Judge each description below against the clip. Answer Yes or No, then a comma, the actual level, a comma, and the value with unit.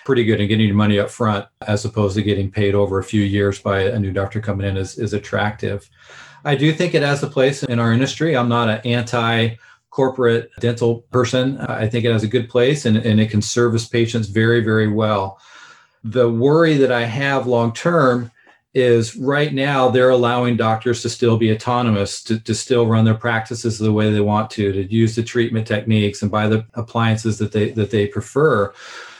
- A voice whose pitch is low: Yes, low, 115 Hz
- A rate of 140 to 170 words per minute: No, fast, 205 wpm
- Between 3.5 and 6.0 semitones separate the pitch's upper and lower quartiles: No, narrow, 2.4 semitones